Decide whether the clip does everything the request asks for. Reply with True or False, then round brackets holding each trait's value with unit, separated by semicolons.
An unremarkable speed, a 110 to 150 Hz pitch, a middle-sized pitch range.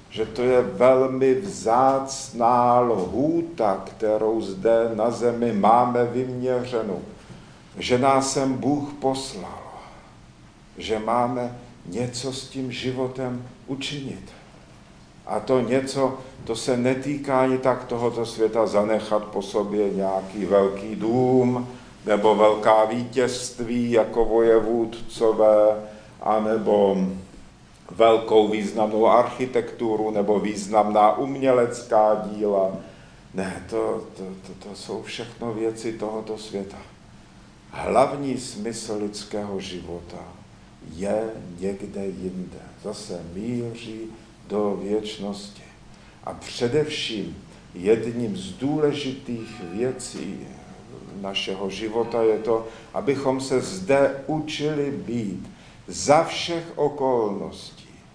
False (95 wpm; 115 Hz; 3.3 semitones)